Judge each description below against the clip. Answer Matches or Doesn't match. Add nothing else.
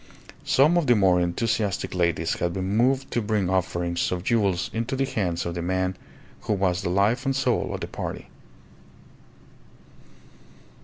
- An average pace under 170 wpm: Matches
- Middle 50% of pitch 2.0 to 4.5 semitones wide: Doesn't match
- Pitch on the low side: Matches